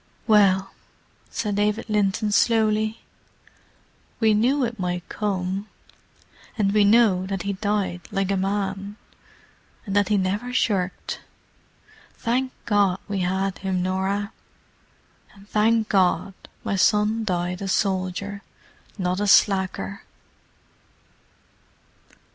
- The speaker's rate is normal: No, slow, 110 wpm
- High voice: Yes, high, 200 Hz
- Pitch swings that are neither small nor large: No, narrow, 2.0 semitones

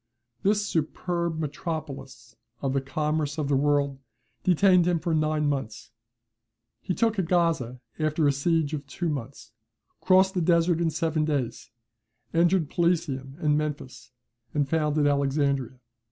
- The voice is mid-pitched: Yes, medium, 155 Hz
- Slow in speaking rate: Yes, slow, 130 wpm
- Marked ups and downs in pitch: No, average, 3.3 semitones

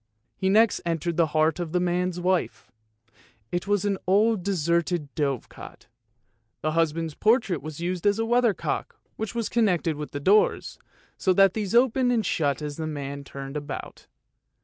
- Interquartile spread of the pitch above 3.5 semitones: Yes, average, 4.7 semitones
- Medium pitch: Yes, medium, 175 Hz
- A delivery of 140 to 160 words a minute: No, average, 170 wpm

